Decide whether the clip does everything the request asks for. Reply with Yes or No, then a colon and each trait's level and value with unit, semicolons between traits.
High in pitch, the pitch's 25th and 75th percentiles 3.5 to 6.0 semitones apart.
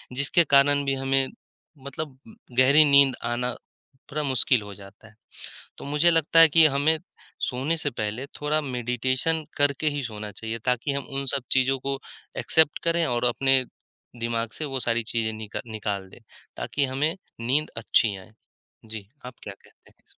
No: low, 135 Hz; average, 3.8 semitones